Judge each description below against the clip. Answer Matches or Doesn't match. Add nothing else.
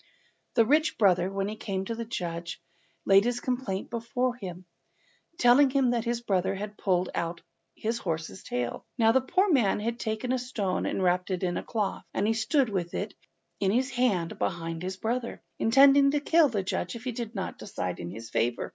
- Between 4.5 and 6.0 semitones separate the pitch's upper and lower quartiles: Matches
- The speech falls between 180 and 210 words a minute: Matches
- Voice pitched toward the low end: Doesn't match